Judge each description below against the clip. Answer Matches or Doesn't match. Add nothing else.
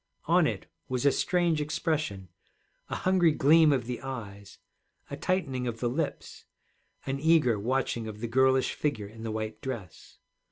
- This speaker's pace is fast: Doesn't match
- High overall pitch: Doesn't match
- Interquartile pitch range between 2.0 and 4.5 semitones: Doesn't match